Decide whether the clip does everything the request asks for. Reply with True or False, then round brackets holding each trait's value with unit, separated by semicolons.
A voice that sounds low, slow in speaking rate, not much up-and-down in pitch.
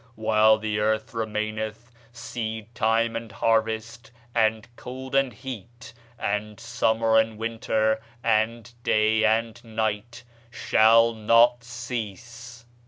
True (110 Hz; 105 wpm; 1.3 semitones)